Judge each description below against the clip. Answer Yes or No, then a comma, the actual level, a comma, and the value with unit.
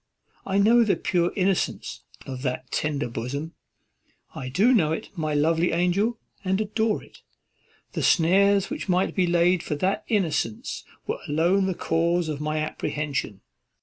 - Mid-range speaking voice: Yes, medium, 175 Hz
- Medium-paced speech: Yes, average, 150 wpm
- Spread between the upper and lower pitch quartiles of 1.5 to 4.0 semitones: No, average, 4.5 semitones